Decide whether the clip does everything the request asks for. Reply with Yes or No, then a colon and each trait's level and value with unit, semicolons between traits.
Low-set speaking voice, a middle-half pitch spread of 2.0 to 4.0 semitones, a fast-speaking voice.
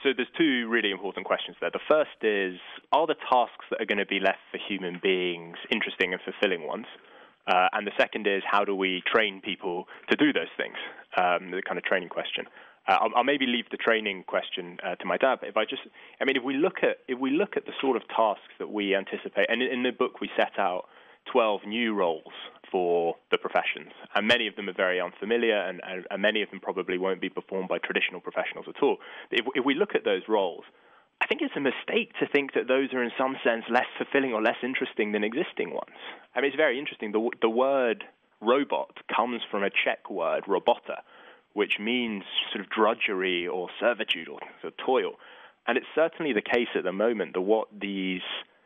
No: low, 115 Hz; wide, 5.4 semitones; fast, 220 wpm